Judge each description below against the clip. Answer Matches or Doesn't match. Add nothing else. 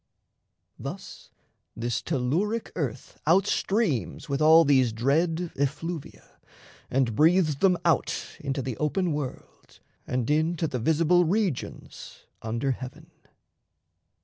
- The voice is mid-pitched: Matches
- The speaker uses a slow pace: Matches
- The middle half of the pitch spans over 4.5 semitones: Matches